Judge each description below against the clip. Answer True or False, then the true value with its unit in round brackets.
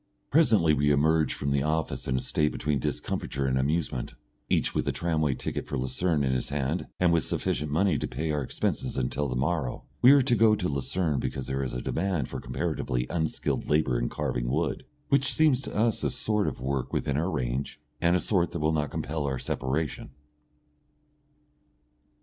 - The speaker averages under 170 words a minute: False (195 wpm)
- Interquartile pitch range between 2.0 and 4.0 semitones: False (4.6 semitones)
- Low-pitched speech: True (75 Hz)